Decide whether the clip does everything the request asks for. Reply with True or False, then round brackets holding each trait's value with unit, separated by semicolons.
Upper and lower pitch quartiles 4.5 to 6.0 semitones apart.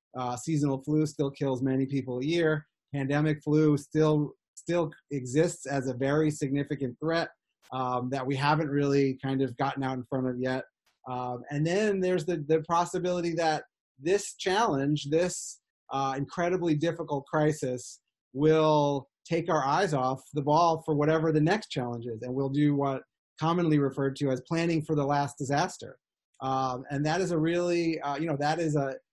False (3.0 semitones)